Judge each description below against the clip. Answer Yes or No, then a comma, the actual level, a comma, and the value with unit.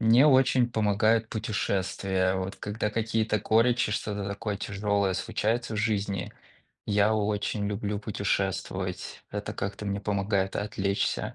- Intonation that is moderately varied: No, narrow, 1.8 semitones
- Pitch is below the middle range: Yes, low, 105 Hz